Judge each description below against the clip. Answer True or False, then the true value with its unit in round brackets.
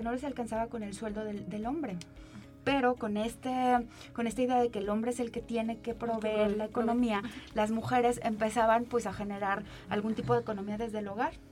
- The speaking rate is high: True (210 wpm)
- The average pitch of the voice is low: False (230 Hz)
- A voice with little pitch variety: True (2.1 semitones)